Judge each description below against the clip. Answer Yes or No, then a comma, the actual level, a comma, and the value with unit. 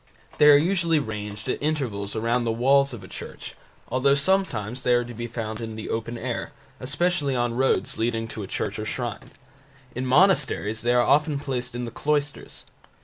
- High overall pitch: No, low, 120 Hz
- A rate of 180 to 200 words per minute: Yes, average, 190 wpm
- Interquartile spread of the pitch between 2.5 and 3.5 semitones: No, average, 4.0 semitones